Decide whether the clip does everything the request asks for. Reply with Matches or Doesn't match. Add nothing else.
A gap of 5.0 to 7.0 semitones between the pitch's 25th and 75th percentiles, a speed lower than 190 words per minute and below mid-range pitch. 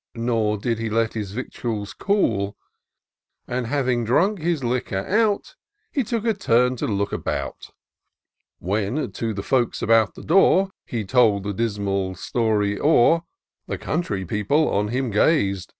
Matches